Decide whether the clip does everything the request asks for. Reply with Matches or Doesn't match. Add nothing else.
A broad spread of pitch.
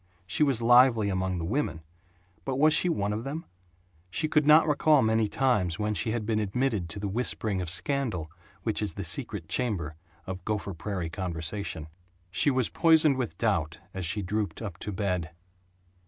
Matches